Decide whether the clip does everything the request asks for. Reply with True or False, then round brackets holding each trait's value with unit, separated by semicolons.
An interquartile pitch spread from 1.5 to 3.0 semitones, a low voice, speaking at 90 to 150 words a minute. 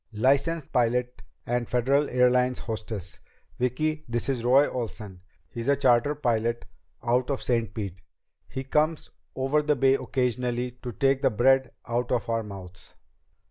True (2.5 semitones; 125 Hz; 145 wpm)